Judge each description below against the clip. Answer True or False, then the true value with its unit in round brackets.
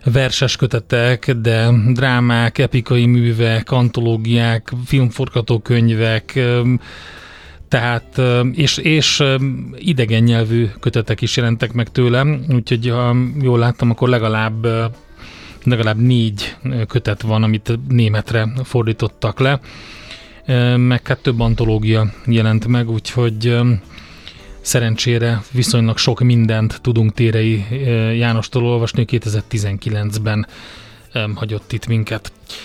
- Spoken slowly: True (95 wpm)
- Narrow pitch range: True (1.8 semitones)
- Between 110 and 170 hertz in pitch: True (120 Hz)